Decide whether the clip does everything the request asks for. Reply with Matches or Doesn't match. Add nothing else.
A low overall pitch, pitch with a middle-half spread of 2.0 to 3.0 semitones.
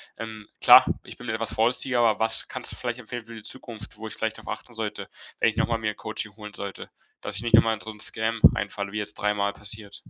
Doesn't match